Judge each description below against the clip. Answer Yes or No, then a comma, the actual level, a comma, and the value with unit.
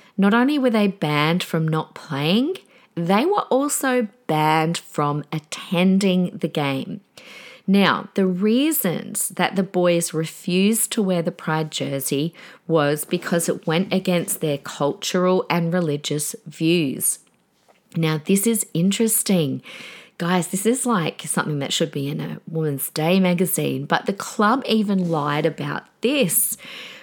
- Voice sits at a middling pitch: Yes, medium, 180 Hz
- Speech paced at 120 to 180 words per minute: Yes, average, 140 wpm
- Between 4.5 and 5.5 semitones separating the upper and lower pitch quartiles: Yes, average, 4.9 semitones